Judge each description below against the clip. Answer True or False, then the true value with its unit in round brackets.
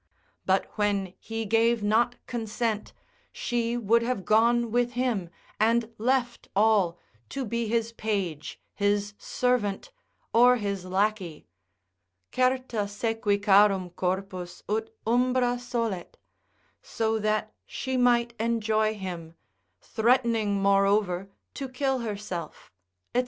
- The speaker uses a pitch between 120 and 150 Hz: False (220 Hz)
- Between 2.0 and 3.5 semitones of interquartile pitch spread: True (3.0 semitones)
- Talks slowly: True (110 wpm)